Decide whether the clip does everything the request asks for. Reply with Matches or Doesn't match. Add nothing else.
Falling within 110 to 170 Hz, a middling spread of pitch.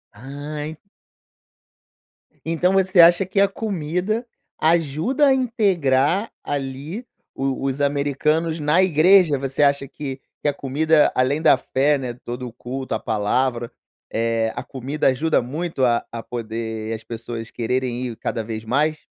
Matches